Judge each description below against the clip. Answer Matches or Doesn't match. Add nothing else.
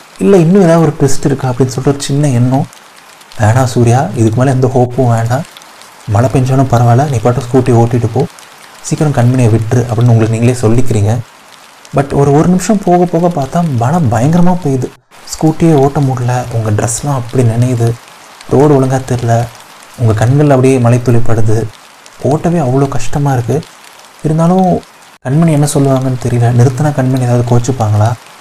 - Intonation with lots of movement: Doesn't match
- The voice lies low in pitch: Matches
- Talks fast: Matches